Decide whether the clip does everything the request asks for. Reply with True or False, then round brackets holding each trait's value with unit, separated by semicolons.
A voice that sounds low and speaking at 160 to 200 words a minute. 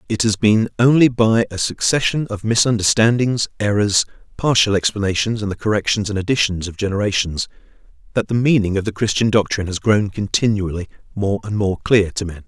True (105 Hz; 170 wpm)